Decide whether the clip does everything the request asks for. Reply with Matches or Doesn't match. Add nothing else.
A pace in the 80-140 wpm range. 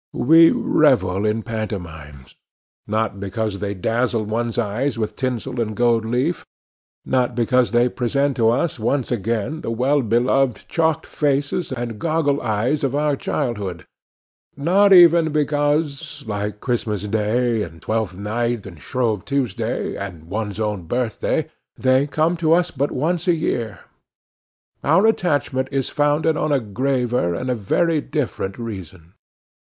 Matches